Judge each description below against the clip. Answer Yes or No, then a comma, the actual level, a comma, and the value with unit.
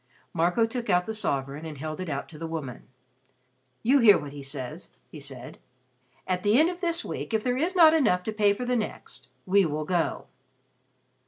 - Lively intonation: Yes, wide, 7.6 semitones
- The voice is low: No, medium, 180 Hz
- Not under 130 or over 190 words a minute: No, average, 200 wpm